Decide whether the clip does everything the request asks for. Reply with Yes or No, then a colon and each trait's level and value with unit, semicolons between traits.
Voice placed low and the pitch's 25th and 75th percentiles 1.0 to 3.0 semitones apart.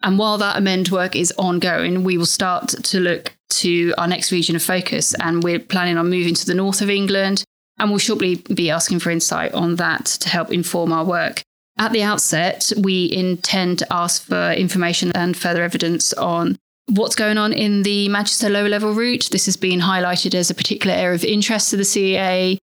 No: medium, 185 Hz; narrow, 2.6 semitones